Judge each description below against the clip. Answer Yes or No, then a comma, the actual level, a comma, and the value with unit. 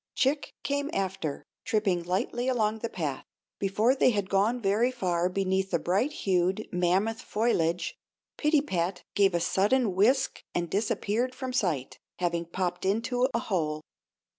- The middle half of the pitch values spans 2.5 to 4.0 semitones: No, average, 5.2 semitones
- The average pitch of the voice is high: Yes, high, 195 Hz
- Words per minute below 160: Yes, average, 140 wpm